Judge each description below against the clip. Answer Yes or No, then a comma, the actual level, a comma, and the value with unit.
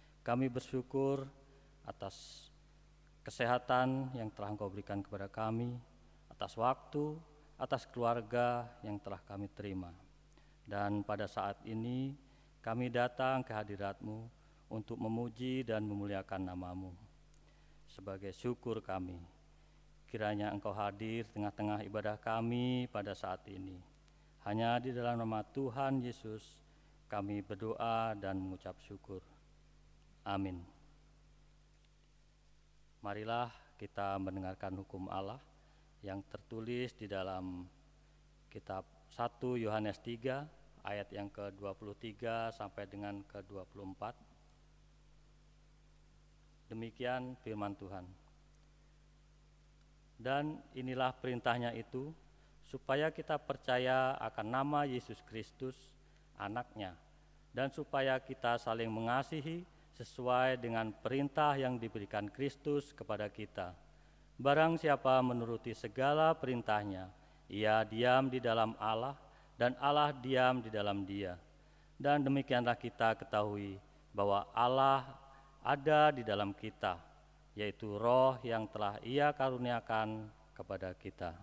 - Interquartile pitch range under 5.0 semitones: Yes, average, 4.3 semitones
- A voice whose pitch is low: Yes, low, 115 Hz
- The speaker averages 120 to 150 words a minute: No, average, 100 wpm